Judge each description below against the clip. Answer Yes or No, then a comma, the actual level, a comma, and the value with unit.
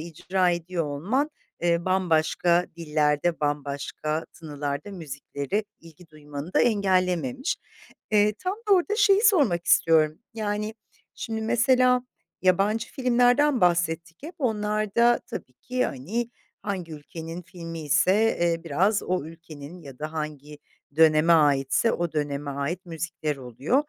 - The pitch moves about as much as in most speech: No, wide, 5.7 semitones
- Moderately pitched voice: Yes, medium, 170 Hz